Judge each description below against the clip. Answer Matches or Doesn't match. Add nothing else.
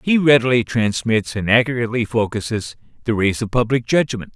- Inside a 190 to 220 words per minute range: Doesn't match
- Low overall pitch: Matches